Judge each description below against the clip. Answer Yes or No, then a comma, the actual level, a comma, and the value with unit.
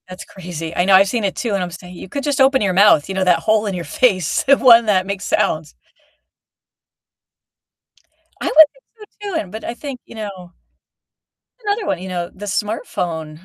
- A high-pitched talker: Yes, high, 195 Hz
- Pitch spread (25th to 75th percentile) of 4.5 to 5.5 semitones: Yes, average, 4.8 semitones